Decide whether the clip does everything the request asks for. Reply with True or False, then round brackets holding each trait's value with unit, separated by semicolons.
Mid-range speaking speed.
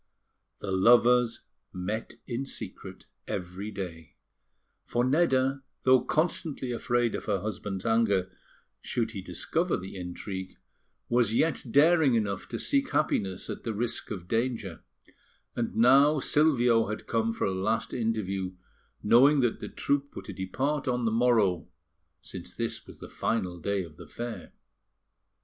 True (145 wpm)